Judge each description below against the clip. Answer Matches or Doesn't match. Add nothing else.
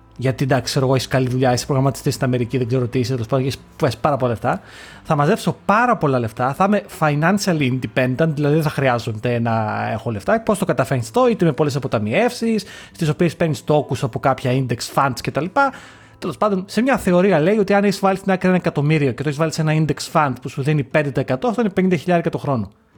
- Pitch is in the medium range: Matches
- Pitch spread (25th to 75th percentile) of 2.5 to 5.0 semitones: Doesn't match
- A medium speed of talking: Doesn't match